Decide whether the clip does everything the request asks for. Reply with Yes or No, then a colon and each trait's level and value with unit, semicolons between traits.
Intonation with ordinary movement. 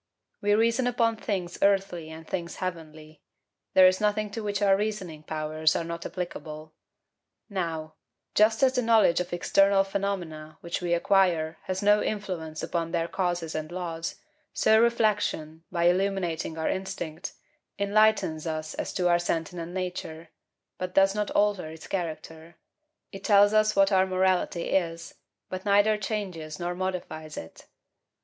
Yes: average, 3.6 semitones